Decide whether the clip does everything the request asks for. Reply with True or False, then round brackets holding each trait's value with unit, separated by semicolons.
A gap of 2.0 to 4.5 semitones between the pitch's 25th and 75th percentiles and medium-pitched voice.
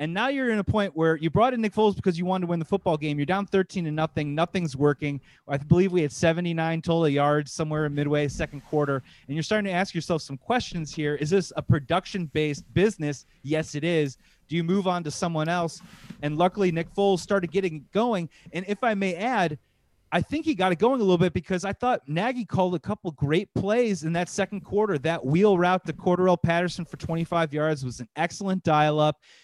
True (4.0 semitones; 170 Hz)